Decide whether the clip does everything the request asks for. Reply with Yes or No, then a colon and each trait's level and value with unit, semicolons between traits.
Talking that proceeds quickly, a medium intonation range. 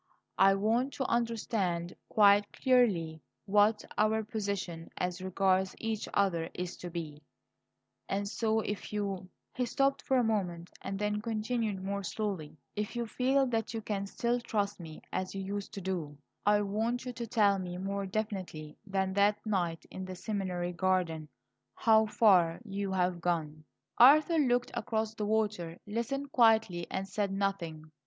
No: average, 160 wpm; average, 3.3 semitones